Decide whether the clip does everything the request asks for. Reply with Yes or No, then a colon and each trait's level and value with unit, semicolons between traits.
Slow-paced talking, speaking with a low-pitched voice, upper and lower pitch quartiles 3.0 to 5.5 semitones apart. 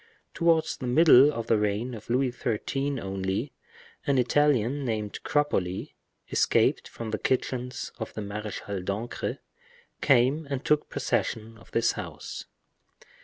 Yes: slow, 130 wpm; low, 120 Hz; average, 4.4 semitones